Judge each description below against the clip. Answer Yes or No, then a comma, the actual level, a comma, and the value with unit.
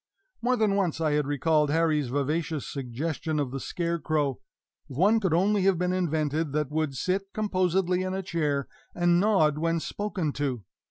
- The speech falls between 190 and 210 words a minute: No, average, 170 wpm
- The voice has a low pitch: No, medium, 165 Hz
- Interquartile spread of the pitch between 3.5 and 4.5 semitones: Yes, average, 4.0 semitones